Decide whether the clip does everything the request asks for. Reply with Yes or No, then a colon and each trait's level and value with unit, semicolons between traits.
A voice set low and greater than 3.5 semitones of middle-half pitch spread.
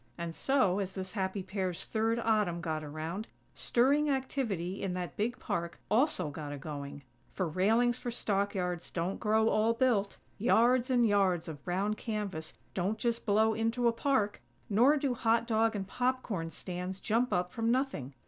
No: high, 205 Hz; average, 4.6 semitones